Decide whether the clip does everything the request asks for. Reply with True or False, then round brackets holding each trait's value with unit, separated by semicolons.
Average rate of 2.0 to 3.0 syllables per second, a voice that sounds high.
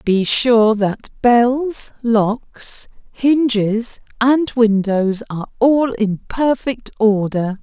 True (2.7 syllables/s; 230 Hz)